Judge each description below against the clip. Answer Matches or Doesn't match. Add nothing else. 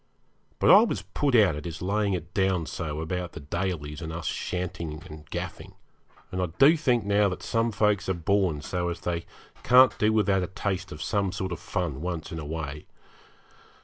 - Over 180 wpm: Matches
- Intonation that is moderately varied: Matches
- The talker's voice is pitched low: Matches